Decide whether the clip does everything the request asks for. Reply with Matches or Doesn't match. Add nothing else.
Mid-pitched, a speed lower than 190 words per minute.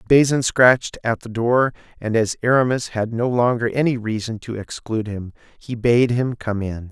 Doesn't match